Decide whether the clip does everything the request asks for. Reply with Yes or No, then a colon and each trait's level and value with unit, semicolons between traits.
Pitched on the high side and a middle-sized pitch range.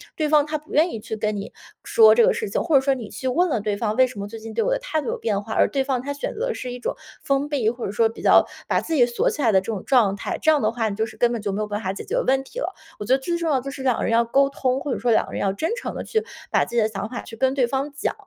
Yes: very high, 255 Hz; average, 4.9 semitones